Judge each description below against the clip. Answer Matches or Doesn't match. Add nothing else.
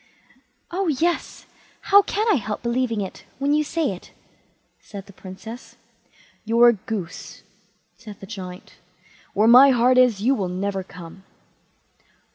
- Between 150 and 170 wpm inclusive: Doesn't match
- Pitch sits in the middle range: Doesn't match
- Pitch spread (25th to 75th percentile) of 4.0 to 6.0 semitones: Matches